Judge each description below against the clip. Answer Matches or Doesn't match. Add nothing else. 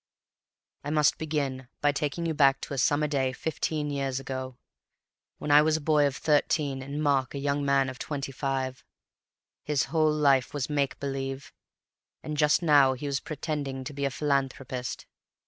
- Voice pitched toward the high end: Doesn't match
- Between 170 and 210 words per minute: Matches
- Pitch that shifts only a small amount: Matches